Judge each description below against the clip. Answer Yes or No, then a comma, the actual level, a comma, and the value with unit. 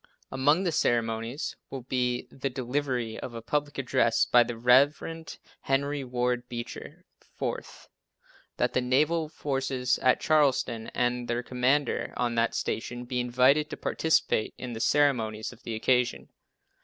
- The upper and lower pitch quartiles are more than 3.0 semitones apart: No, narrow, 2.5 semitones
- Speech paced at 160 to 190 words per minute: No, average, 145 wpm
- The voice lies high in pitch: No, low, 125 Hz